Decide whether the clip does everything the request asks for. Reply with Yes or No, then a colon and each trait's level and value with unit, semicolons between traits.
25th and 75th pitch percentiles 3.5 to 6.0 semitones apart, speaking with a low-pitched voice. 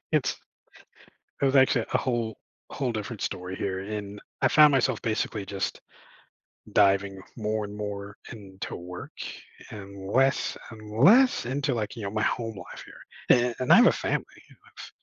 Yes: average, 3.9 semitones; low, 110 Hz